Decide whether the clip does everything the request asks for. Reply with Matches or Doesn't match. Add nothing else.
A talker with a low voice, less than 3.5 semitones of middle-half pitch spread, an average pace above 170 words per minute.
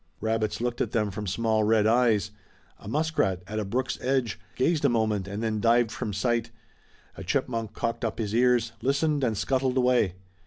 Matches